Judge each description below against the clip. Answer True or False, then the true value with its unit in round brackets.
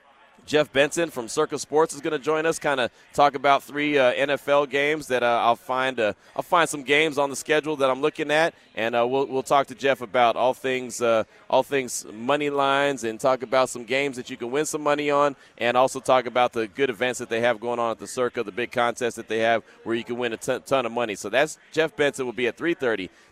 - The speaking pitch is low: True (130 Hz)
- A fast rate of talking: True (255 wpm)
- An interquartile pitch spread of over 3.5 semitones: False (3.2 semitones)